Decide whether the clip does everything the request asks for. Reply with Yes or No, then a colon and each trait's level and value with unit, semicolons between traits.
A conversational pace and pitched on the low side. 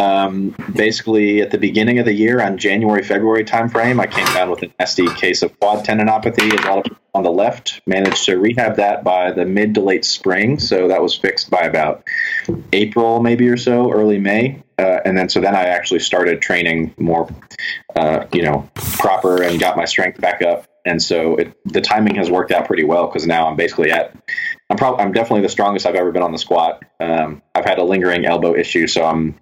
No: fast, 220 wpm; low, 100 Hz